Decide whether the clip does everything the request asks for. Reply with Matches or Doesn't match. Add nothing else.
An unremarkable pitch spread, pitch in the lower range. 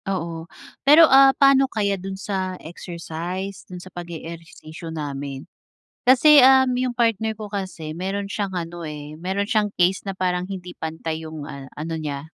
Doesn't match